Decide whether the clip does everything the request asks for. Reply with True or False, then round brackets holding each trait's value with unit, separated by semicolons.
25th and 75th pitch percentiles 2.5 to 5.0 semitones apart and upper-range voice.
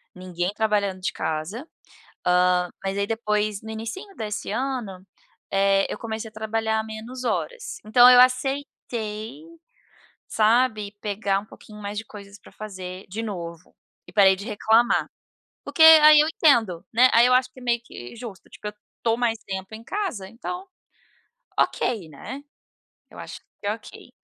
True (3.6 semitones; 220 Hz)